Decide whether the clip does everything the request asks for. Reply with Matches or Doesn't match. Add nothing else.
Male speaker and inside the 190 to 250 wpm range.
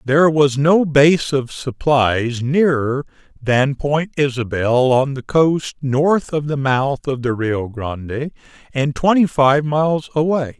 Doesn't match